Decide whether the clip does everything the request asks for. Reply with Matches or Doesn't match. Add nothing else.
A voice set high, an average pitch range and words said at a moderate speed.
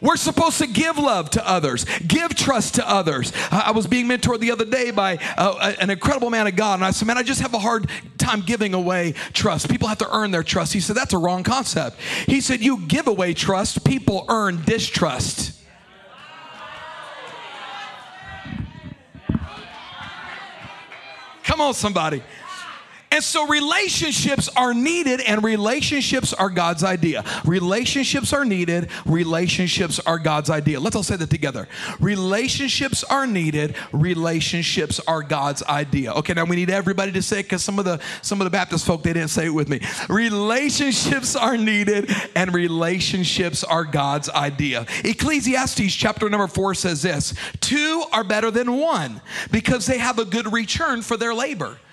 Doesn't match